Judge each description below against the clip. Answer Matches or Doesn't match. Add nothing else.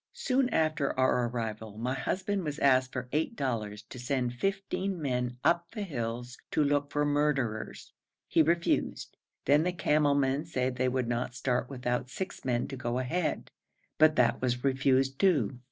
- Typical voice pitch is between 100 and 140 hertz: Matches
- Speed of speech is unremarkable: Matches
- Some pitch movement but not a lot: Matches